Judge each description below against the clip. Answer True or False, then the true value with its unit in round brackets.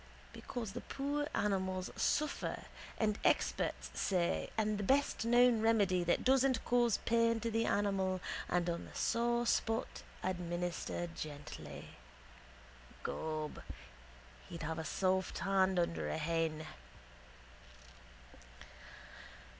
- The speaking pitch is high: True (195 Hz)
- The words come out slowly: True (110 wpm)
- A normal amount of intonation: True (5.0 semitones)